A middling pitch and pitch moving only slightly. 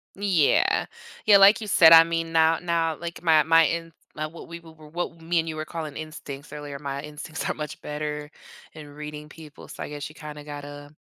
Yes: medium, 155 Hz; narrow, 1.9 semitones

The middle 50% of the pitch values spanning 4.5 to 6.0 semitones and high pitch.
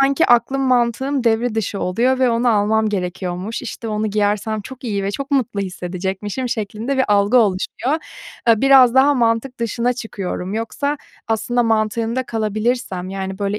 No: average, 3.6 semitones; high, 225 Hz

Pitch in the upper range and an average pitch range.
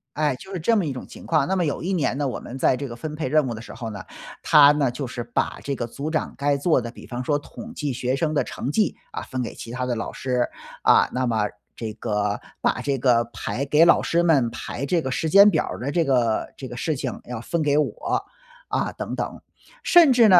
No: medium, 140 Hz; average, 4.3 semitones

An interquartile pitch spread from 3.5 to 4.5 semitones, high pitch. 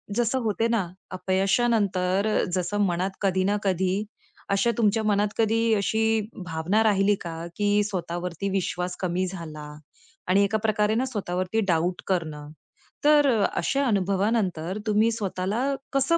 No: average, 3.1 semitones; high, 200 Hz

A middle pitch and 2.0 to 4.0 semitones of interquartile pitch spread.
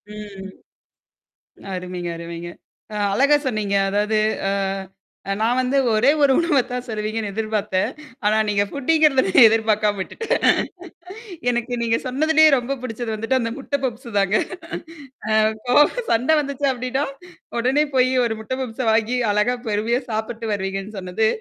No: high, 225 Hz; average, 3.5 semitones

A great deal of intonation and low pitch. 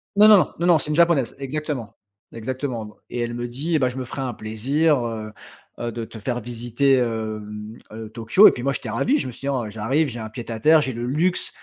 No: average, 4.5 semitones; low, 120 Hz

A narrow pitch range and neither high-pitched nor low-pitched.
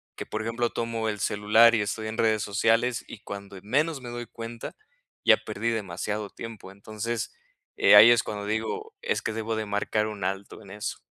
No: narrow, 2.0 semitones; low, 110 Hz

